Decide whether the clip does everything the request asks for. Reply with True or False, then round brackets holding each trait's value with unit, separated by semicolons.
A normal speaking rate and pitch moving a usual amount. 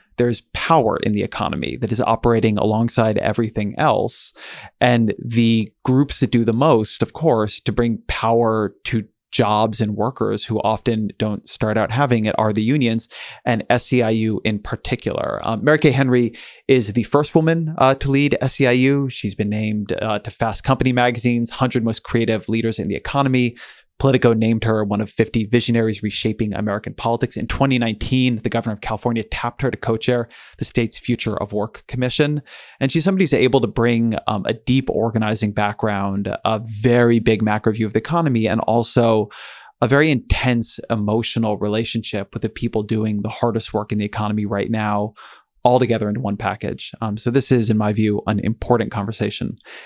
False (180 wpm; 2.3 semitones)